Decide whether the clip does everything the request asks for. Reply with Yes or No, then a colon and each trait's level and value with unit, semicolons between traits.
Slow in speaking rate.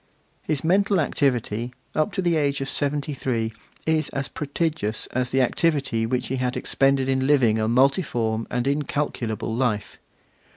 No: average, 155 wpm